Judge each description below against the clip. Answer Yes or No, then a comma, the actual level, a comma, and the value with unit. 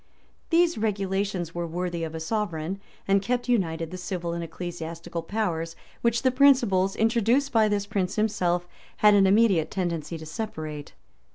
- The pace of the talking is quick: No, average, 160 wpm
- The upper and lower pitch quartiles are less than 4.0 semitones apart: No, average, 4.5 semitones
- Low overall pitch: No, high, 190 Hz